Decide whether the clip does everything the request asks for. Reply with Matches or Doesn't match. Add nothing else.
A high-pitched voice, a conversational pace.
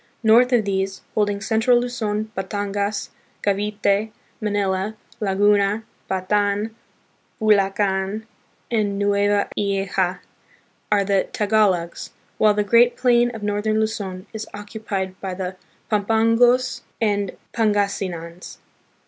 Doesn't match